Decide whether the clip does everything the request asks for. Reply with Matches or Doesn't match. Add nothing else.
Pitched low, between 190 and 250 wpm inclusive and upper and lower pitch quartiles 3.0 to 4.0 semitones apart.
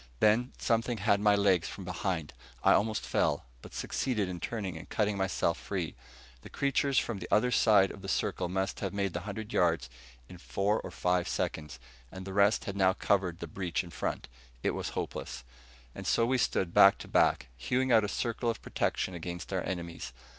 Matches